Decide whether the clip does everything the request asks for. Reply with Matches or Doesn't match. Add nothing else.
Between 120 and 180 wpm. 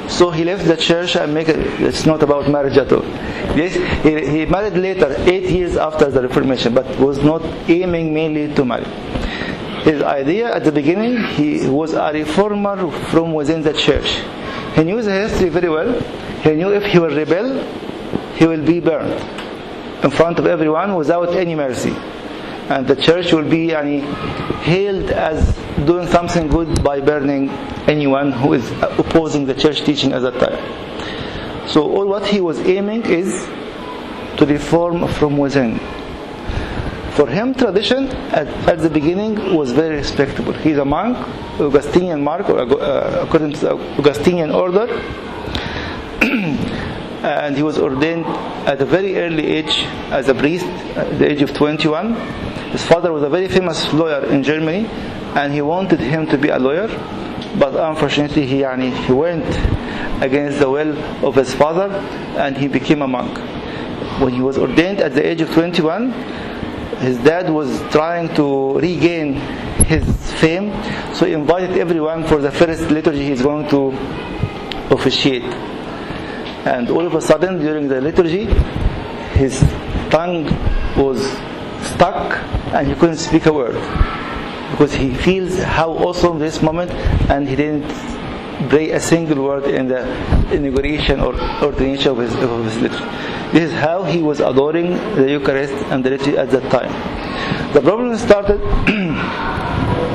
Matches